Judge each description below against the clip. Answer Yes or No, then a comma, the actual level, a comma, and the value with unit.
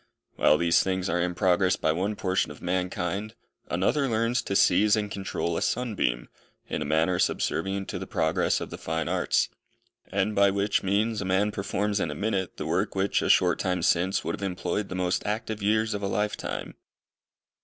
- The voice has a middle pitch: No, very low, 95 Hz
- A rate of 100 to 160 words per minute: No, average, 195 wpm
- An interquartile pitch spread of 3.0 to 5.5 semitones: No, narrow, 2.6 semitones